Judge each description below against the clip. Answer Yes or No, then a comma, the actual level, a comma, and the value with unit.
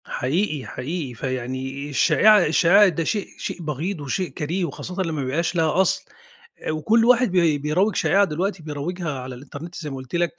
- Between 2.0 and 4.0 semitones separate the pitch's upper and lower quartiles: No, average, 4.6 semitones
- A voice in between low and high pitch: Yes, medium, 160 Hz